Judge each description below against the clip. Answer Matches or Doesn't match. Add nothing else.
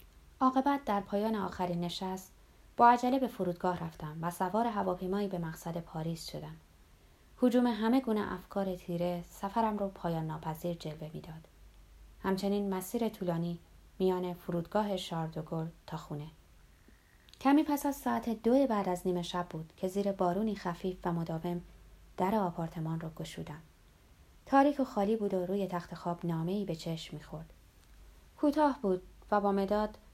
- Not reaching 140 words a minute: Doesn't match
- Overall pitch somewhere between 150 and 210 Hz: Matches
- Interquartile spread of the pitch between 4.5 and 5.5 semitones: Doesn't match